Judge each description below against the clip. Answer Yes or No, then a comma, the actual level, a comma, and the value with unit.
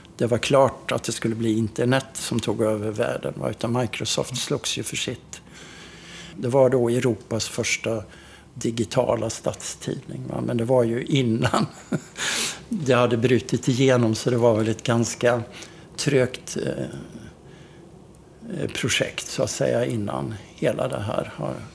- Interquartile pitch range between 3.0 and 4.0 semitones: No, narrow, 2.5 semitones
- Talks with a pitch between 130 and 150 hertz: No, low, 120 Hz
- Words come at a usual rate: Yes, average, 135 wpm